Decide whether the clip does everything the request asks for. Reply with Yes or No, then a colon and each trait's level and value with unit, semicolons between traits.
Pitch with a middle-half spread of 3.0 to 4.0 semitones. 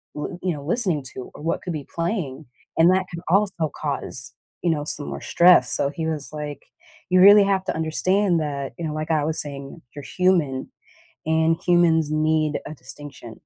Yes: average, 3.3 semitones